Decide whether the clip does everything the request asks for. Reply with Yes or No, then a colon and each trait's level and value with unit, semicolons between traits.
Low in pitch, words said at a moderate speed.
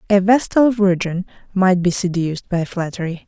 No: high, 190 Hz; average, 145 wpm